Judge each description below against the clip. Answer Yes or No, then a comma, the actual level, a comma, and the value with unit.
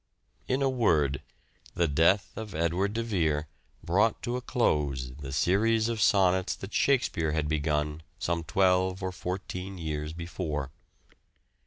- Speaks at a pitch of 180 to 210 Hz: No, very low, 90 Hz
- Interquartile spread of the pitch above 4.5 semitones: Yes, average, 5.0 semitones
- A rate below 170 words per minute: Yes, average, 140 wpm